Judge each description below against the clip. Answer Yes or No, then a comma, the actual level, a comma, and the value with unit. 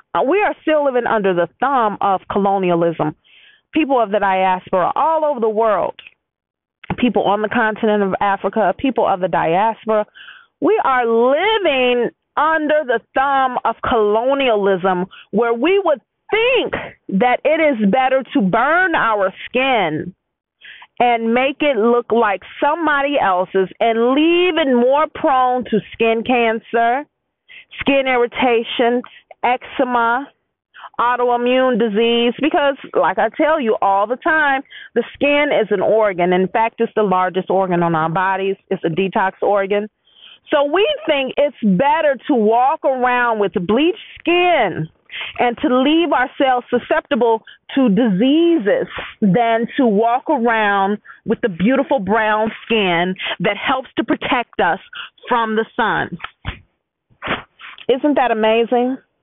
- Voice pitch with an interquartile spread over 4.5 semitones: Yes, average, 5.1 semitones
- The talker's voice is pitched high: Yes, high, 240 Hz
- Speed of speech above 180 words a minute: No, slow, 135 wpm